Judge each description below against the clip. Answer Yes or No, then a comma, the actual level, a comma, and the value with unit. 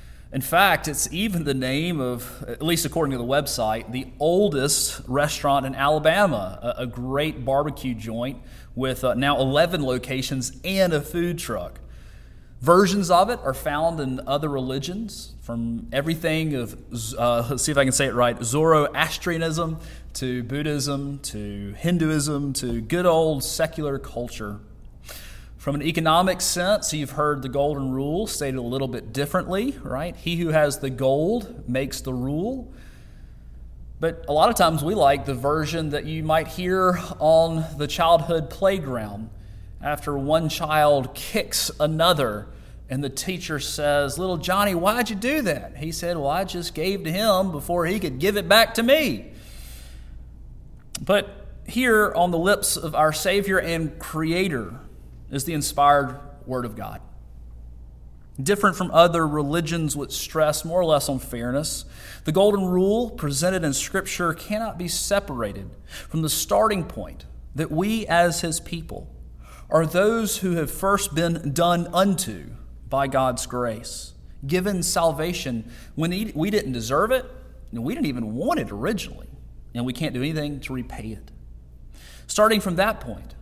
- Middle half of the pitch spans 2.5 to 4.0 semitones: No, average, 5.1 semitones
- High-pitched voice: No, medium, 150 Hz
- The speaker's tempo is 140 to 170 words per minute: Yes, average, 155 wpm